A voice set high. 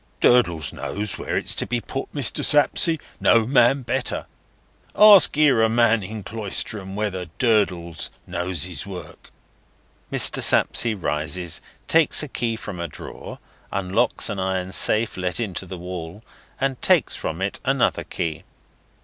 No: low, 105 Hz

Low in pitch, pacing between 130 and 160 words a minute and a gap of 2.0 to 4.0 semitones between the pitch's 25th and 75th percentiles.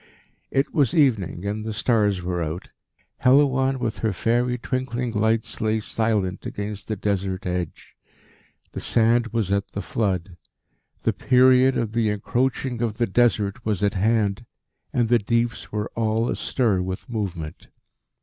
Yes: low, 110 Hz; average, 150 wpm; average, 3.3 semitones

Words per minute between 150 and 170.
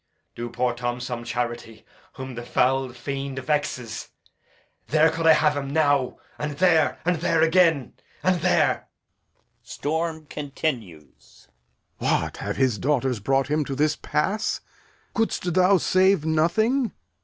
No: slow, 135 wpm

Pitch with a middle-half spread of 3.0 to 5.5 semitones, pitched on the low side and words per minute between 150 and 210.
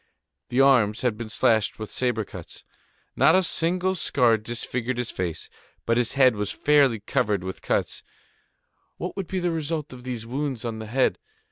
Yes: average, 4.7 semitones; low, 125 Hz; average, 175 wpm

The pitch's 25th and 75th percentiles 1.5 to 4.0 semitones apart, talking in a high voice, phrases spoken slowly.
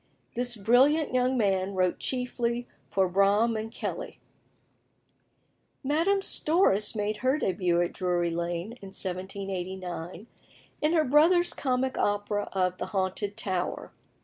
No: average, 5.3 semitones; high, 205 Hz; slow, 120 wpm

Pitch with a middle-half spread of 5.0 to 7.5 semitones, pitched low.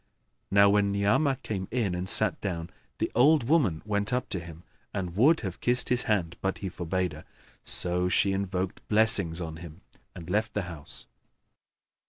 No: average, 3.6 semitones; very low, 95 Hz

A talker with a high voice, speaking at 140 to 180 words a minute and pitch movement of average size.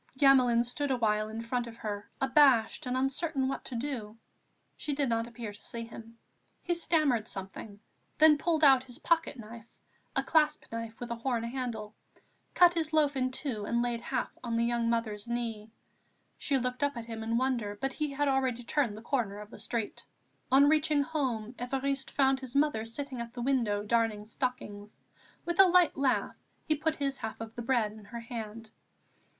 No: high, 245 Hz; average, 190 wpm; average, 3.5 semitones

